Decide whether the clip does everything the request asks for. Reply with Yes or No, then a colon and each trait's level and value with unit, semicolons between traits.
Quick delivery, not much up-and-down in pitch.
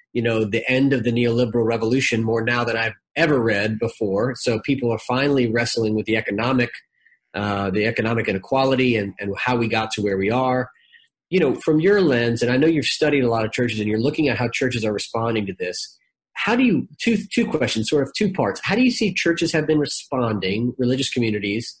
No: fast, 220 wpm; average, 4.3 semitones